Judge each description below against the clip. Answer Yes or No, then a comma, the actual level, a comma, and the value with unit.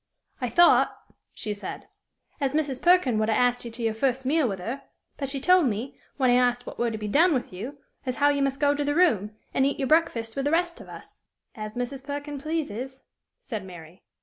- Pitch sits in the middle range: No, very high, 265 Hz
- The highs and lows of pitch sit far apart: No, average, 4.2 semitones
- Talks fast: Yes, fast, 230 wpm